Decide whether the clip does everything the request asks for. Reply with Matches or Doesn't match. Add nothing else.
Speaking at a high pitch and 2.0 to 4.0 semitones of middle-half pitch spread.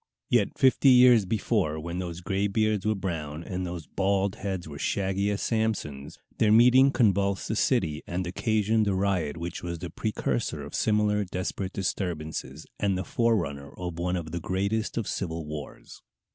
Doesn't match